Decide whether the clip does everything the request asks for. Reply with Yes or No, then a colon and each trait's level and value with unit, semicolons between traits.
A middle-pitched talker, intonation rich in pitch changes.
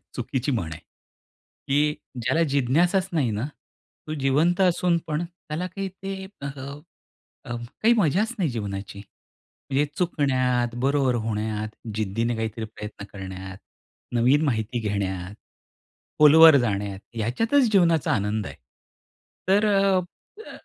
No: low, 130 Hz; wide, 7.9 semitones